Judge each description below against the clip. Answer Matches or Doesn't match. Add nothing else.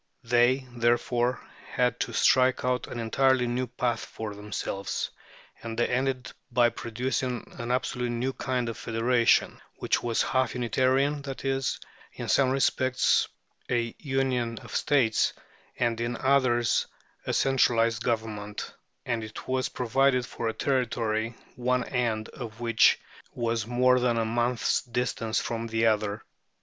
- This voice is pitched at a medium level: Doesn't match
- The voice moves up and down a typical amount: Doesn't match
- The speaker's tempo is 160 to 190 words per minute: Doesn't match